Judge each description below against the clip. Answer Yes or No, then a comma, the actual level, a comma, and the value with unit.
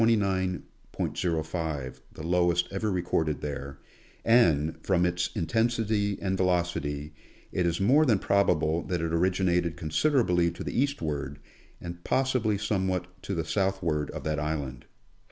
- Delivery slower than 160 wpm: Yes, slow, 135 wpm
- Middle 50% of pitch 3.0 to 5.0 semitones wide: Yes, average, 3.9 semitones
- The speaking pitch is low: Yes, very low, 90 Hz